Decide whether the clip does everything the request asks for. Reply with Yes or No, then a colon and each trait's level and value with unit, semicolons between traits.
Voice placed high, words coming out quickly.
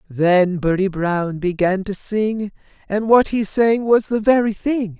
No: high, 200 Hz; average, 170 wpm